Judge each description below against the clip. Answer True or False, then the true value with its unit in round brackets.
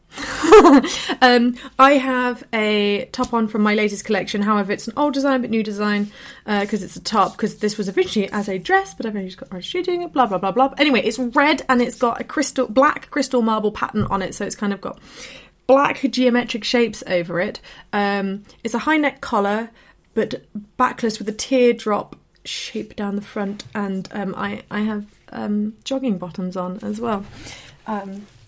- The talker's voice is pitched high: True (215 Hz)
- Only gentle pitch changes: False (3.9 semitones)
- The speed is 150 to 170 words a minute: False (190 wpm)